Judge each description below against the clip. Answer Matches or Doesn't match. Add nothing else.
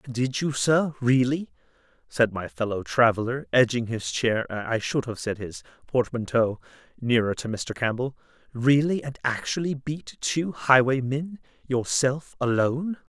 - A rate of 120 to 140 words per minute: Matches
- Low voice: Matches